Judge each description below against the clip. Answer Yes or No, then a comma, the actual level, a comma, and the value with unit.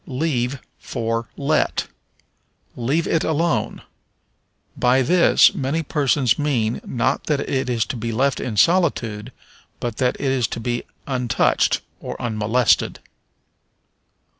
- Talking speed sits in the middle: No, slow, 120 wpm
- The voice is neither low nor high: No, low, 125 Hz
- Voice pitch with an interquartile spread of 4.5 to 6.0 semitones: No, average, 3.7 semitones